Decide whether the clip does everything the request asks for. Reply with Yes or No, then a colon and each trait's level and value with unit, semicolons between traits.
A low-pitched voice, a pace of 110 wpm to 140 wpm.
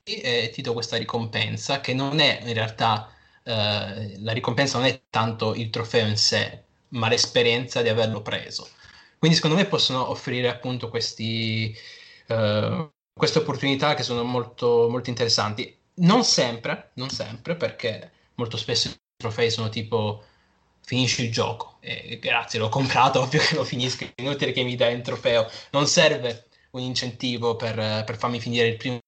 No: low, 120 Hz; average, 160 wpm